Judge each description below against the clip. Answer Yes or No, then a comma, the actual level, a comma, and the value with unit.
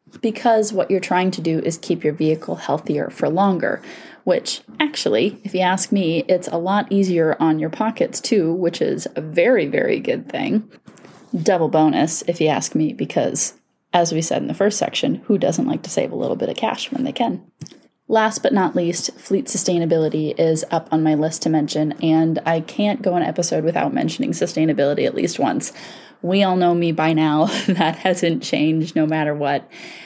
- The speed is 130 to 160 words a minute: No, average, 195 wpm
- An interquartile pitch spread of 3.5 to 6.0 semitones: Yes, average, 4.0 semitones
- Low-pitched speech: No, medium, 170 Hz